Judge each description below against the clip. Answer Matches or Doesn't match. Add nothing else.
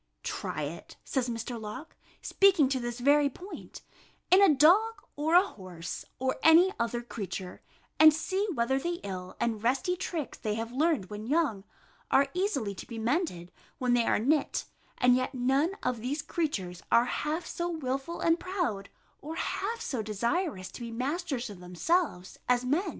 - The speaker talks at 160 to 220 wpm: Matches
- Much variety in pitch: Matches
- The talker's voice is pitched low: Doesn't match